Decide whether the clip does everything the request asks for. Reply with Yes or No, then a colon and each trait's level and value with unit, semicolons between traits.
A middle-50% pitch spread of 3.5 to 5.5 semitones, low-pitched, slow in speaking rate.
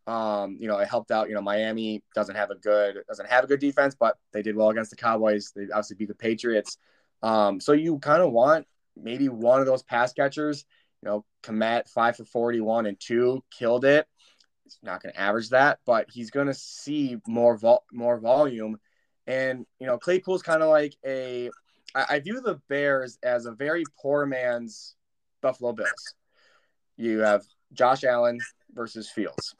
No: average, 4.3 semitones; low, 120 Hz; average, 190 wpm